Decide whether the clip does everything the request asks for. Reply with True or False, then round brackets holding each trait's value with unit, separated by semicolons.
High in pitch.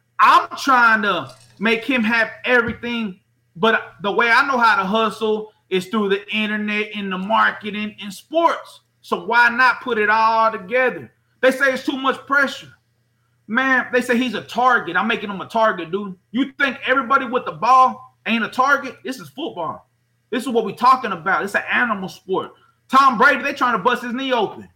True (225 Hz)